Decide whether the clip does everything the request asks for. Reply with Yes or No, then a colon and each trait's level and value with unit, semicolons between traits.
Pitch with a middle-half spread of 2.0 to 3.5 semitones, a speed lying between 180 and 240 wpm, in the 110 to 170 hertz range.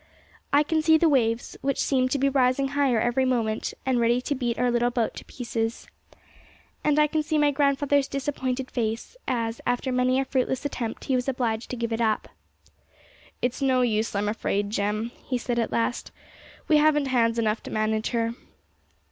No: average, 3.1 semitones; average, 190 wpm; very high, 250 Hz